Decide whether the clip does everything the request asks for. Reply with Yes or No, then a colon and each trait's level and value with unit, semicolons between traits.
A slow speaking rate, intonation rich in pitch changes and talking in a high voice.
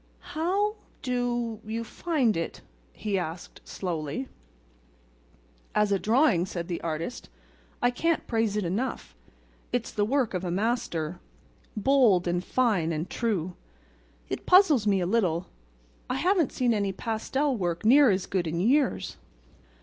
Yes: slow, 130 wpm; wide, 6.0 semitones; high, 215 Hz